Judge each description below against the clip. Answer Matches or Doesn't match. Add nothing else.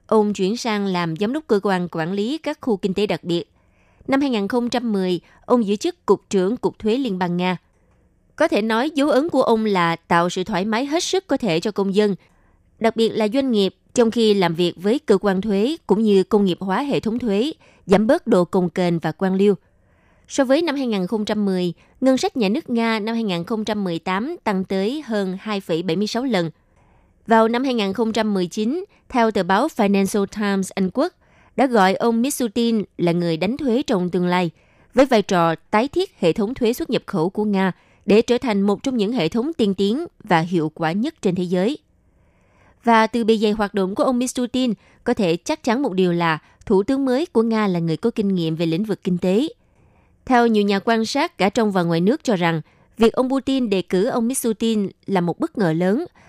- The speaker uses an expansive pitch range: Doesn't match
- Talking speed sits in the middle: Matches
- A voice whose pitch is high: Matches